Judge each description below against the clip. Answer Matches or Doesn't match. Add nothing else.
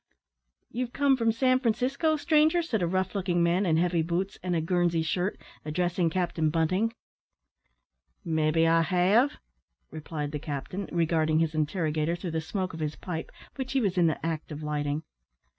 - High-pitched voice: Doesn't match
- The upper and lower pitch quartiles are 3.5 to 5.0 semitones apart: Matches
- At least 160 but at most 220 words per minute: Matches